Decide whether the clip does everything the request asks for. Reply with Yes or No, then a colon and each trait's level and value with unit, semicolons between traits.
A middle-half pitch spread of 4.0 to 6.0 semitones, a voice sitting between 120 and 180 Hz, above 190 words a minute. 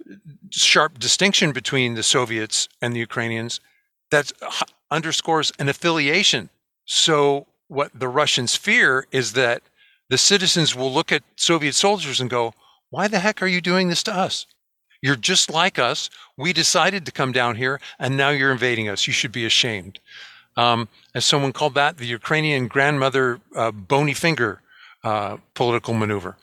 No: wide, 5.6 semitones; medium, 140 Hz; average, 160 wpm